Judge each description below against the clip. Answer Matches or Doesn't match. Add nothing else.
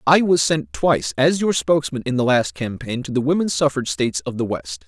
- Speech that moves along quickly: Matches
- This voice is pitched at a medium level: Matches